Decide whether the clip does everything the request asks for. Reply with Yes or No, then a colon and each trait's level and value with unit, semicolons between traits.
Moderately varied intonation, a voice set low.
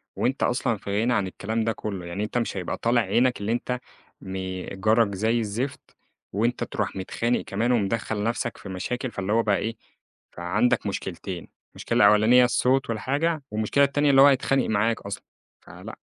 Yes: average, 3.5 semitones; low, 115 Hz